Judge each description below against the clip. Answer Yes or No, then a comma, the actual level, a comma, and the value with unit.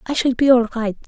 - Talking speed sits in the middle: No, fast, 280 wpm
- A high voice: Yes, high, 245 Hz